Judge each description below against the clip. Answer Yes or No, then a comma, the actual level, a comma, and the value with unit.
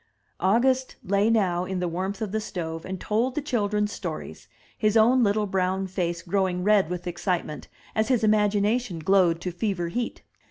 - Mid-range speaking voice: No, high, 200 Hz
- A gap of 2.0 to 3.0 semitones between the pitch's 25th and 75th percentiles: No, average, 3.4 semitones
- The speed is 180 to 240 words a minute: No, average, 170 wpm